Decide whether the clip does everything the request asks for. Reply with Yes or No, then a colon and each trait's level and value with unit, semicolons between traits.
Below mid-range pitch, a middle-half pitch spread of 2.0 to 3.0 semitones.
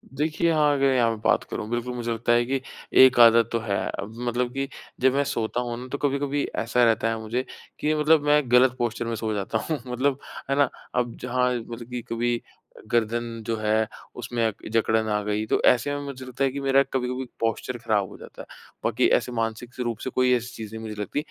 Yes: low, 120 Hz; narrow, 2.5 semitones